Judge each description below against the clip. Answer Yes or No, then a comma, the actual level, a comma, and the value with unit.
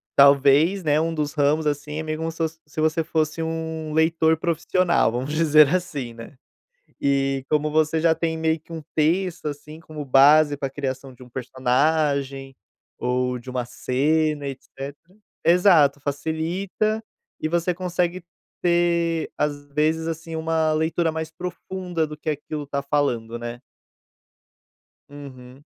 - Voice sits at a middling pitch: Yes, medium, 155 Hz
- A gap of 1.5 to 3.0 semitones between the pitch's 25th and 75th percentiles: Yes, narrow, 2.6 semitones